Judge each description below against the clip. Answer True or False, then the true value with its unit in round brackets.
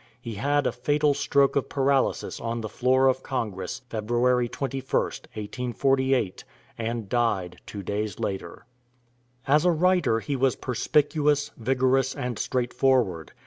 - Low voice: True (125 Hz)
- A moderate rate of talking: False (130 wpm)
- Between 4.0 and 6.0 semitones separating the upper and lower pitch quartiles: False (3.4 semitones)